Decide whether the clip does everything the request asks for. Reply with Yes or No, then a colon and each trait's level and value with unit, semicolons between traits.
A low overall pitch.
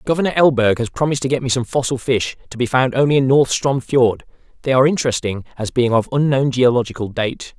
Yes: low, 130 Hz